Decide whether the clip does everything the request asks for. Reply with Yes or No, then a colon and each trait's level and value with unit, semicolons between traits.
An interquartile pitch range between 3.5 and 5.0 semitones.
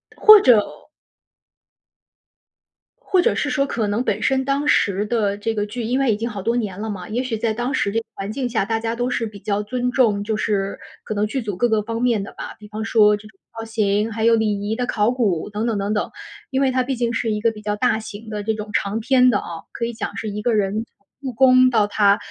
No: average, 2.7 semitones